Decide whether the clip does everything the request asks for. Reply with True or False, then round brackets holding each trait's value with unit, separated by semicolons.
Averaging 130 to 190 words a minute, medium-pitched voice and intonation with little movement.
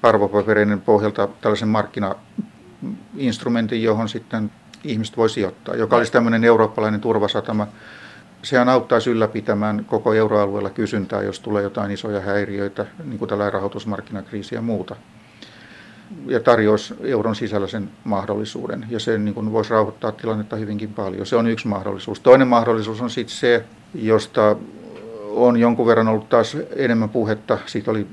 False (135 wpm; 110 Hz; 1.8 semitones)